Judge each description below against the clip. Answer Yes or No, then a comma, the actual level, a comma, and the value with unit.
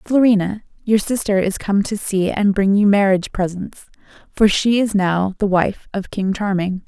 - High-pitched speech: Yes, high, 200 Hz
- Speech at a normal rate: Yes, average, 185 wpm